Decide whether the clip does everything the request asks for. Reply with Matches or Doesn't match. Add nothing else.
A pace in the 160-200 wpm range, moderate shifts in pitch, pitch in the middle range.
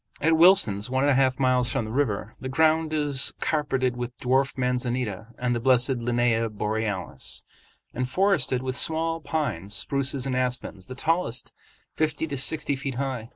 Doesn't match